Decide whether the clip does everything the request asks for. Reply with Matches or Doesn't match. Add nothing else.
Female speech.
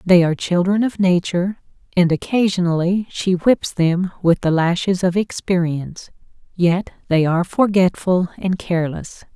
Matches